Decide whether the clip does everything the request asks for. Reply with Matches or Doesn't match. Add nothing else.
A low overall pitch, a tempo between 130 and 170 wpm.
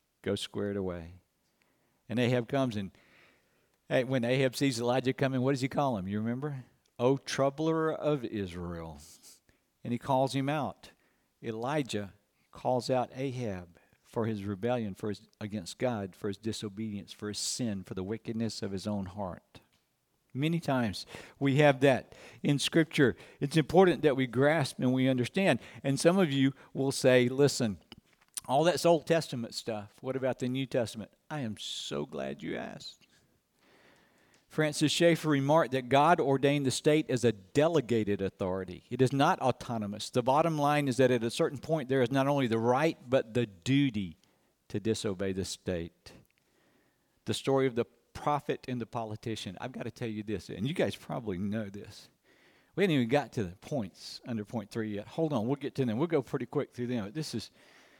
Doesn't match